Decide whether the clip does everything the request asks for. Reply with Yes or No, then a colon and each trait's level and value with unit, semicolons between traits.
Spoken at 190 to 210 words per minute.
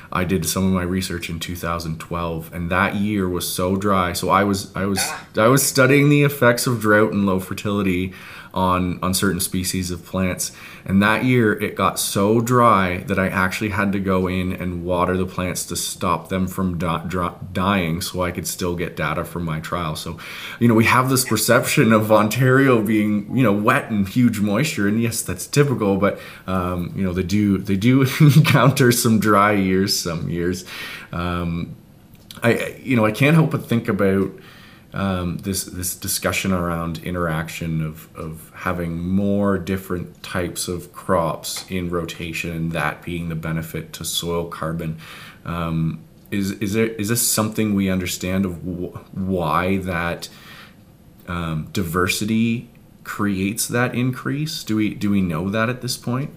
No: average, 175 wpm